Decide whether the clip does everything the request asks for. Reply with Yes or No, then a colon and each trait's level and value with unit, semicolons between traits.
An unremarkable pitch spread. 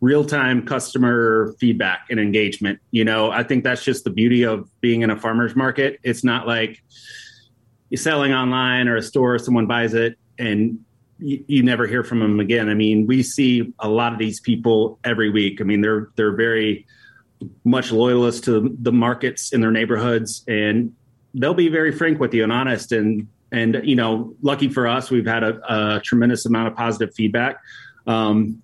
No: narrow, 2.1 semitones